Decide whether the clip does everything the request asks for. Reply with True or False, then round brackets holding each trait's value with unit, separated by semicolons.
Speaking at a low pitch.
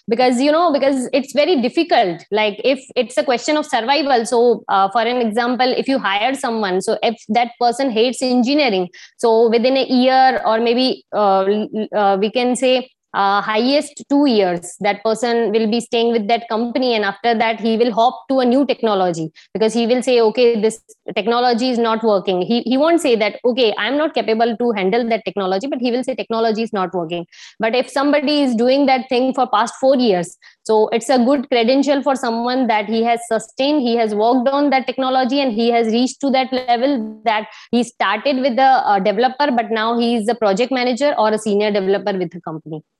False (235 Hz)